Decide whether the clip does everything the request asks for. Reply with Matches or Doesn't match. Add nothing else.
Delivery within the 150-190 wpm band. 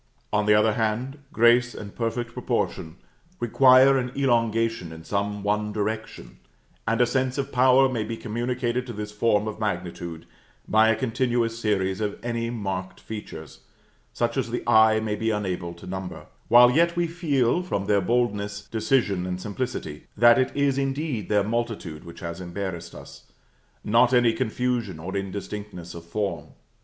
Matches